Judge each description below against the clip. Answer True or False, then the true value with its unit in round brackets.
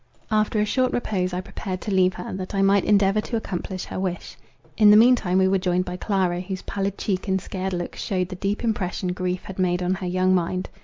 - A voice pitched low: False (190 Hz)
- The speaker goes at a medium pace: False (240 wpm)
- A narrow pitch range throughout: True (1.8 semitones)